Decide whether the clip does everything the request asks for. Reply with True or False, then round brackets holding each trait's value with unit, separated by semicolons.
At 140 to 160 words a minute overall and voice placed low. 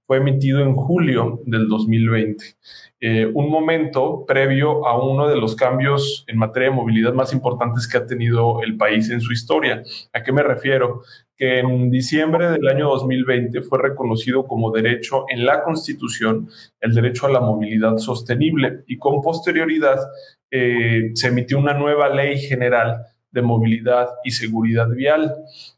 True (155 wpm; 125 Hz)